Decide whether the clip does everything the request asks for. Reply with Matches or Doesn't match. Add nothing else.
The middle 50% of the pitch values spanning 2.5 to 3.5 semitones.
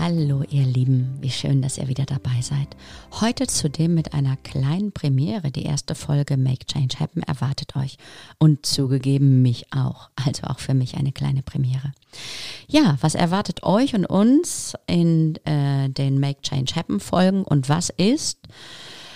Matches